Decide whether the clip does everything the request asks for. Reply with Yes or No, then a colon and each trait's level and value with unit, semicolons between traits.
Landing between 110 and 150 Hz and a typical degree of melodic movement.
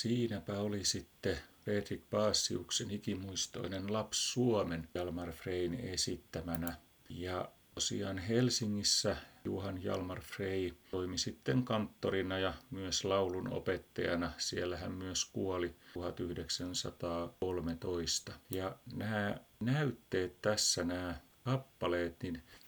No: very low, 95 Hz; average, 3.2 semitones